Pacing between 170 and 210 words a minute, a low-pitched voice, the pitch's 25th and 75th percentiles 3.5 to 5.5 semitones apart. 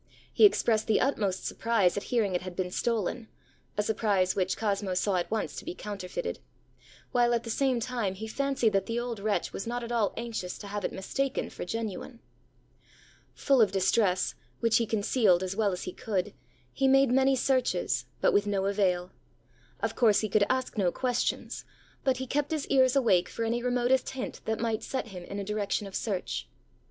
No: average, 195 wpm; high, 220 Hz; average, 3.9 semitones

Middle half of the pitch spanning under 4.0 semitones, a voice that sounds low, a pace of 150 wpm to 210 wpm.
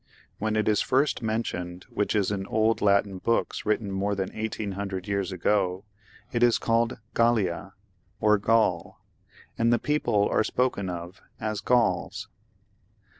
No: average, 2.8 semitones; low, 105 Hz; average, 140 wpm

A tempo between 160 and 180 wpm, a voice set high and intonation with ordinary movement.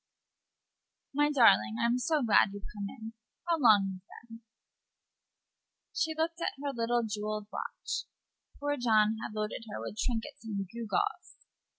No: average, 145 wpm; high, 230 Hz; average, 4.9 semitones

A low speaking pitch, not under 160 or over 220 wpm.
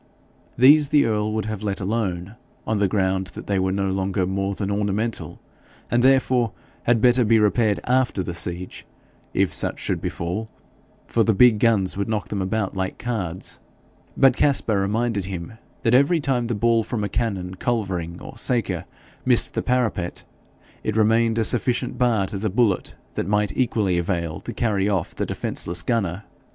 Yes: low, 105 Hz; average, 175 wpm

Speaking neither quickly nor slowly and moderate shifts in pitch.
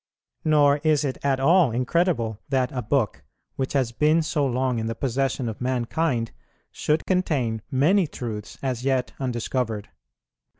Yes: average, 145 wpm; average, 4.0 semitones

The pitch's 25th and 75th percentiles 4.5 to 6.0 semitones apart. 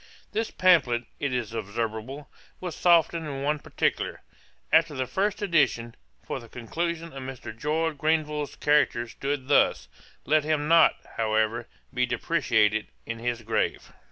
Yes: average, 5.2 semitones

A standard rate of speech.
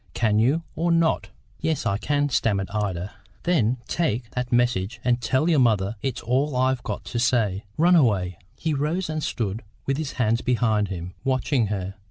Yes: average, 180 wpm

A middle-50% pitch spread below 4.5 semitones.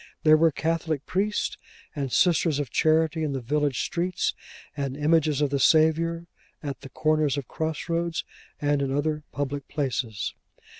Yes: narrow, 2.5 semitones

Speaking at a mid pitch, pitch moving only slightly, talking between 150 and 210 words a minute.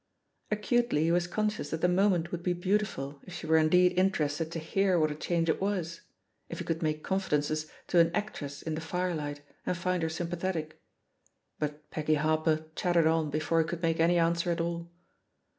Yes: medium, 165 Hz; narrow, 2.3 semitones; average, 195 wpm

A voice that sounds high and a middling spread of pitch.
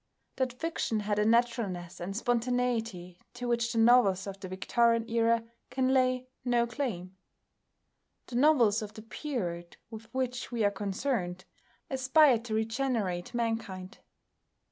Yes: high, 230 Hz; average, 3.6 semitones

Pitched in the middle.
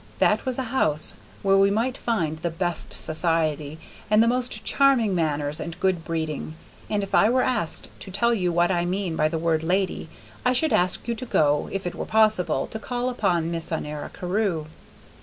Yes: medium, 180 Hz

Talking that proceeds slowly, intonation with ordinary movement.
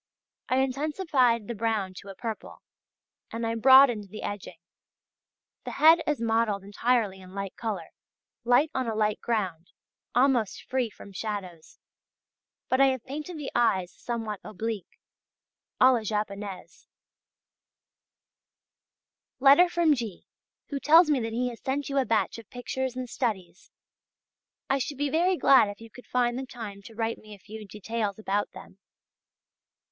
No: average, 150 wpm; average, 4.3 semitones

